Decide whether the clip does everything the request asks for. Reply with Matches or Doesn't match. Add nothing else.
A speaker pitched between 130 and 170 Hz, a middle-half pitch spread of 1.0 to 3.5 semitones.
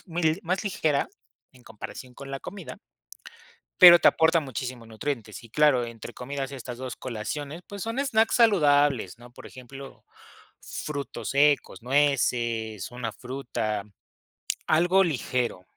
Doesn't match